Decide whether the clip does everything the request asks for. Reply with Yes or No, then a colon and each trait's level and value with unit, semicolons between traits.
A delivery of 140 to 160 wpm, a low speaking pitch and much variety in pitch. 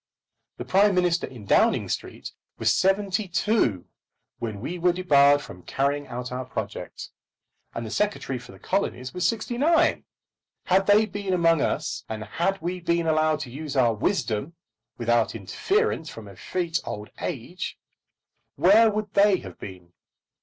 No: average, 155 wpm; medium, 165 Hz; wide, 8.0 semitones